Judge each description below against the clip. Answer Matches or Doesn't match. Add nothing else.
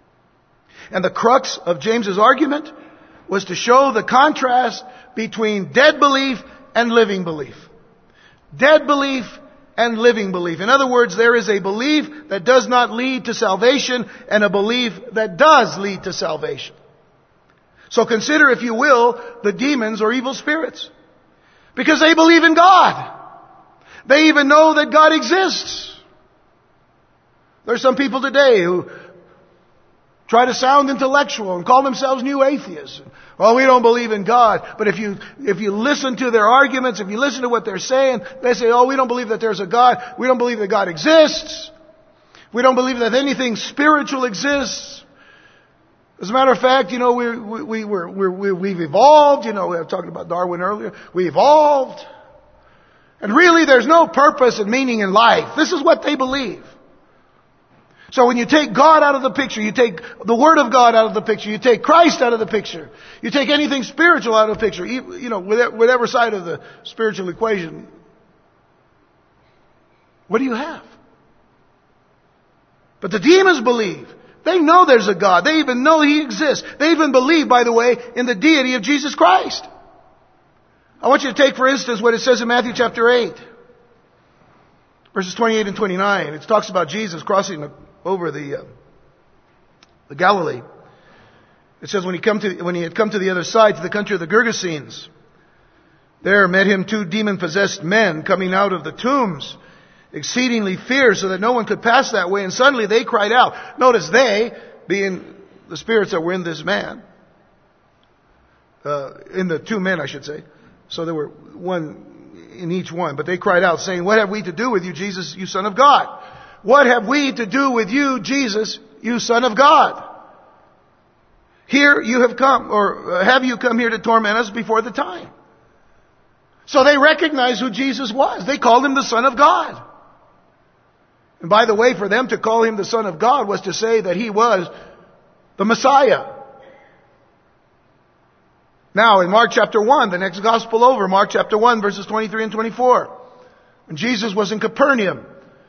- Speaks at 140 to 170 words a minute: Doesn't match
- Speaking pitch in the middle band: Doesn't match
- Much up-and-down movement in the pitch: Doesn't match